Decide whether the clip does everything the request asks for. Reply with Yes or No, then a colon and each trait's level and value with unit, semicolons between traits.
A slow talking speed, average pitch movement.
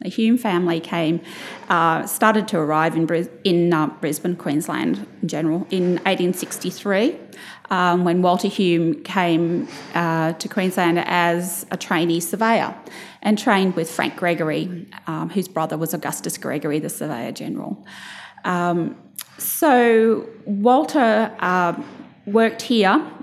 Yes: slow, 130 wpm; average, 3.5 semitones